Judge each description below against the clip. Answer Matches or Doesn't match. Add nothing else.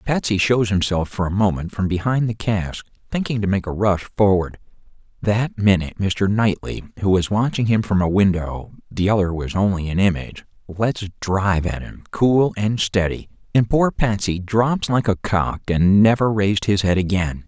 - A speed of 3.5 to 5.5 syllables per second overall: Matches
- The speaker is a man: Matches